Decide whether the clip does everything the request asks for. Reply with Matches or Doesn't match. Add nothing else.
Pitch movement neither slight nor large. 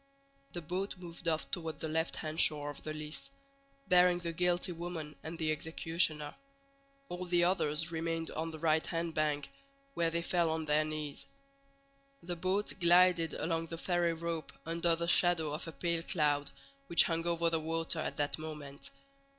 Doesn't match